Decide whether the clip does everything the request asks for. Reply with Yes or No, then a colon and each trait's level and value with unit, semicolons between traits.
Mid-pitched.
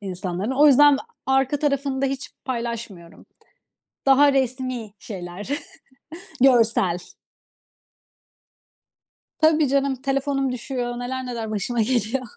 No: very high, 255 Hz